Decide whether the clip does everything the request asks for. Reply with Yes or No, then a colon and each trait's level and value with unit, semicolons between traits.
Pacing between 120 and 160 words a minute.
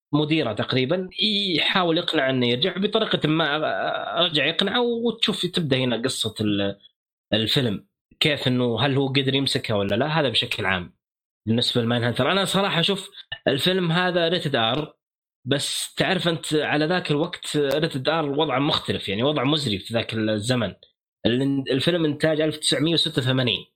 Yes: fast, 135 wpm